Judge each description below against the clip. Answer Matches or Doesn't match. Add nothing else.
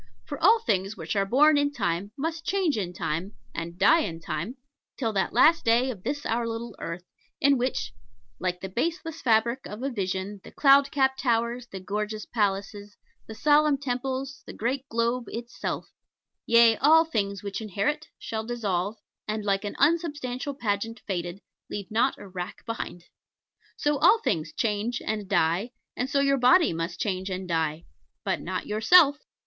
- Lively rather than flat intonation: Matches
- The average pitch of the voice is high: Matches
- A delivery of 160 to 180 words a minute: Matches